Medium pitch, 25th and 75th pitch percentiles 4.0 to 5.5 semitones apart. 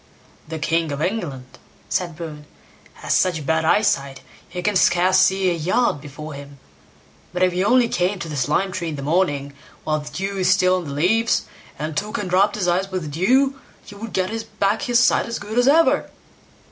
Yes: medium, 180 Hz; average, 4.8 semitones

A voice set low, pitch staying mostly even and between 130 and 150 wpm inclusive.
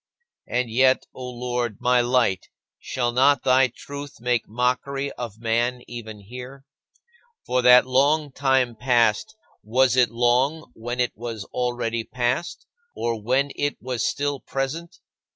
Yes: low, 125 Hz; narrow, 2.0 semitones; slow, 135 wpm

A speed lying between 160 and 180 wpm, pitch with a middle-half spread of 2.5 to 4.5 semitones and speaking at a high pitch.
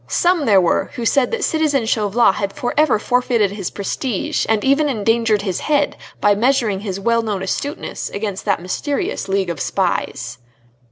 No: average, 170 wpm; average, 5.1 semitones; high, 220 Hz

